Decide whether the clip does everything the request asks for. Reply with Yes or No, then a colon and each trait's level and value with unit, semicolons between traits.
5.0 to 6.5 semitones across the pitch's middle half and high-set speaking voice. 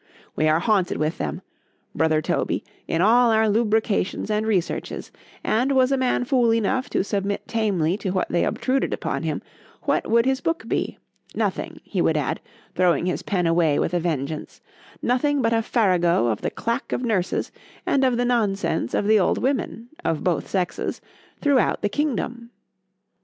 Yes: wide, 5.6 semitones; high, 215 Hz